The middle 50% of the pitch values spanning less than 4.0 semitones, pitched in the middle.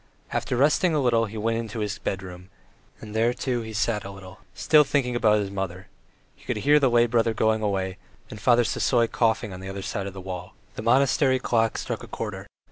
No: average, 3.6 semitones; low, 110 Hz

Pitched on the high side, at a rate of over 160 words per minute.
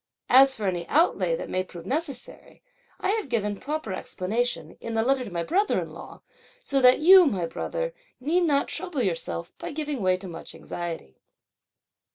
Yes: high, 240 Hz; average, 180 wpm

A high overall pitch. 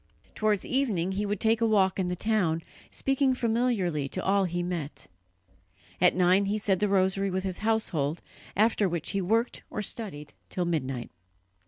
Yes: high, 195 Hz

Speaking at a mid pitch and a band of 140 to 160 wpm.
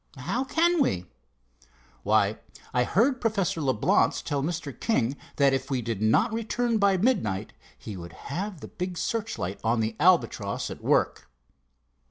Yes: medium, 160 Hz; average, 150 wpm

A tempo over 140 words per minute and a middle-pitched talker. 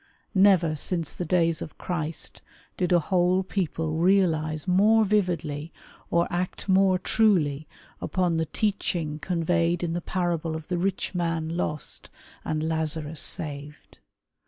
No: slow, 135 wpm; medium, 170 Hz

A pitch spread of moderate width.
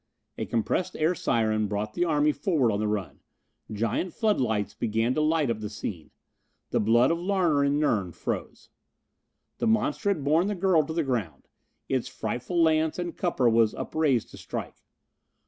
No: wide, 7.1 semitones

